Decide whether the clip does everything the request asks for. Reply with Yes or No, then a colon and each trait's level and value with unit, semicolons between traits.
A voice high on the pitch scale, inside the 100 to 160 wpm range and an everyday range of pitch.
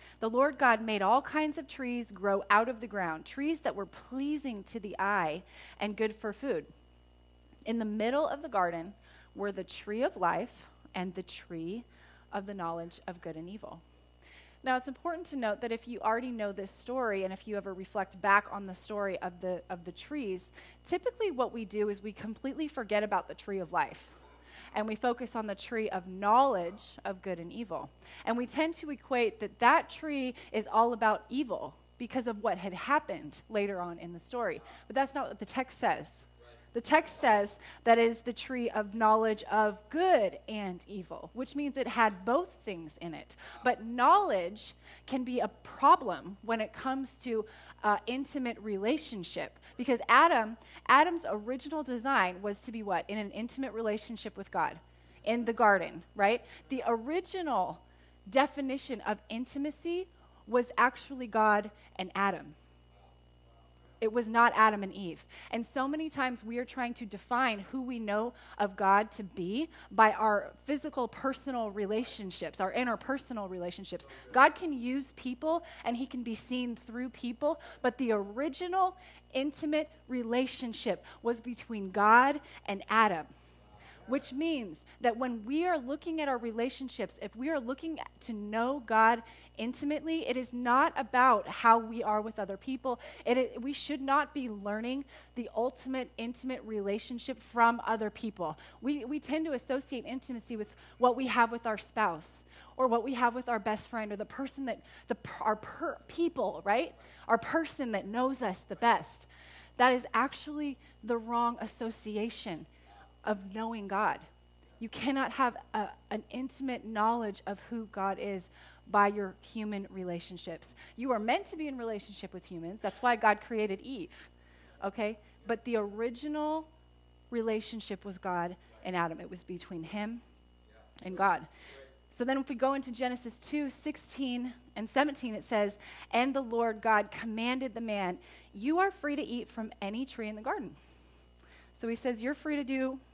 No: high, 230 Hz; average, 170 wpm; average, 4.4 semitones